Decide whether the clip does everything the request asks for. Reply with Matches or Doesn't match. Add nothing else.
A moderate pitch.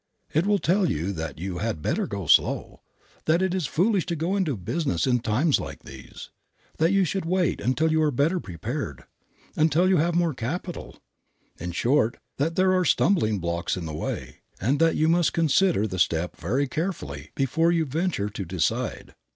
Matches